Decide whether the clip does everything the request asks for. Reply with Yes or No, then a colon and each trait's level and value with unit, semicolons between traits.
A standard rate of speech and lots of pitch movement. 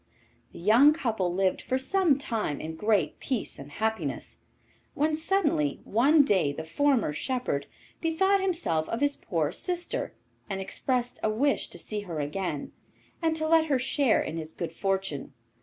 Yes: average, 160 wpm; wide, 8.9 semitones